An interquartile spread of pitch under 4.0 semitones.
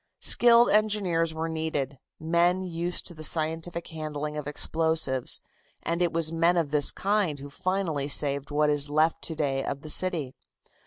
Yes: average, 2.8 semitones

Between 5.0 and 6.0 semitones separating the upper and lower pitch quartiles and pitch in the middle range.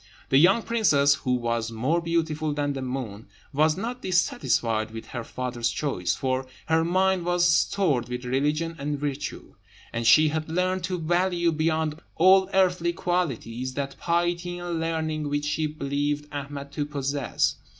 No: average, 4.3 semitones; medium, 150 Hz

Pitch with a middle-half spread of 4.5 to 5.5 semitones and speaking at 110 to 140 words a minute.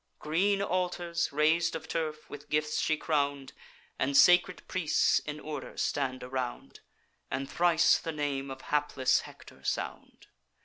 No: average, 3.2 semitones; slow, 135 wpm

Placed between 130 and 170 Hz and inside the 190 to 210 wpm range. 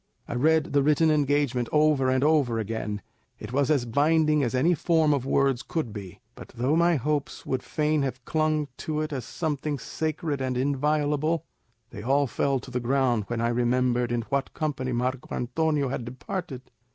No: medium, 140 Hz; average, 180 wpm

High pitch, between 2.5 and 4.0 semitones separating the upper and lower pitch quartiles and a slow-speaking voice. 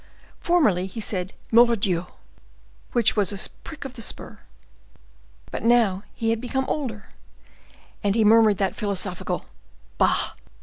Yes: high, 220 Hz; average, 3.5 semitones; slow, 130 wpm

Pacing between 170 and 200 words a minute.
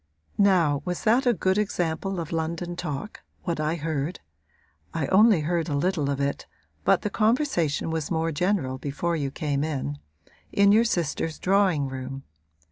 No: average, 160 wpm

